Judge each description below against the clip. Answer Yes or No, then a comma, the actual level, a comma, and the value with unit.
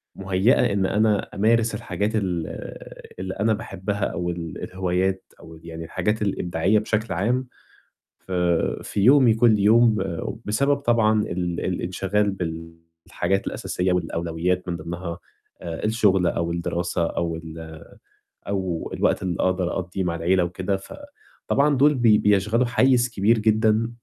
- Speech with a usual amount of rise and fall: Yes, average, 3.9 semitones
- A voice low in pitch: Yes, very low, 95 Hz